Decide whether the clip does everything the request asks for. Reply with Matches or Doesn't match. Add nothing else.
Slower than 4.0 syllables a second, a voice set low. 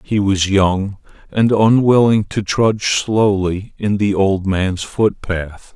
Matches